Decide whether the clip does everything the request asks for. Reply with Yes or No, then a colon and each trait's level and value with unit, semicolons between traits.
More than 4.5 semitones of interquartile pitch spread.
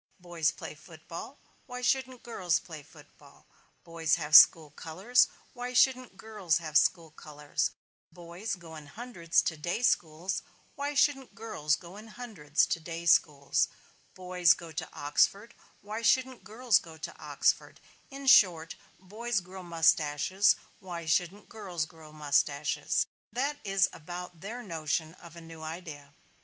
Yes: wide, 5.5 semitones